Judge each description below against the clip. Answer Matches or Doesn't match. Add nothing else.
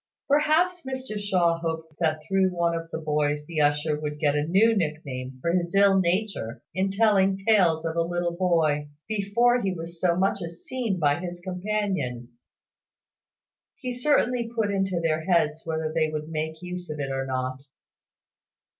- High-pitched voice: Doesn't match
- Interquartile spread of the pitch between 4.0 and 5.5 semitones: Matches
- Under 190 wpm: Matches